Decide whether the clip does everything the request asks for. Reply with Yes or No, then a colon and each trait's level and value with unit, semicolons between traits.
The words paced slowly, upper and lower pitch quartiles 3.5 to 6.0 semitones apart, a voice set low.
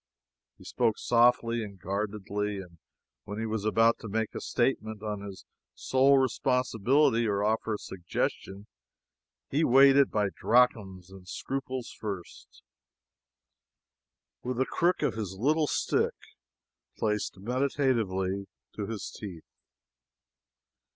Yes: slow, 120 wpm; average, 4.1 semitones; low, 110 Hz